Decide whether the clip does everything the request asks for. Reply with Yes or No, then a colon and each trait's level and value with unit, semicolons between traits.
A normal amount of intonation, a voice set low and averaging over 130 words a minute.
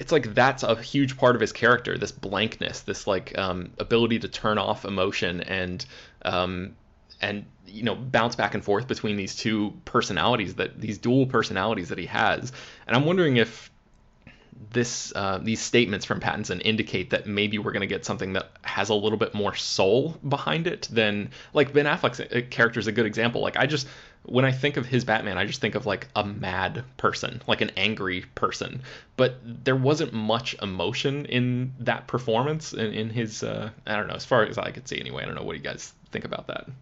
Yes: average, 3.4 semitones; low, 110 Hz; fast, 205 wpm